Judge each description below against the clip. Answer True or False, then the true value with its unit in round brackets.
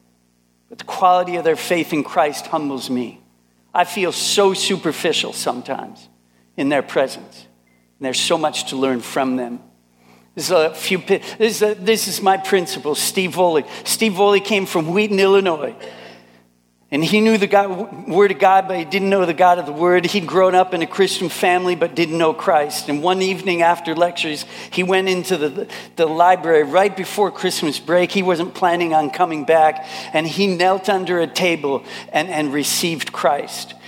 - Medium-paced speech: True (180 wpm)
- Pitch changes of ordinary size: True (4.5 semitones)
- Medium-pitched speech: True (175 Hz)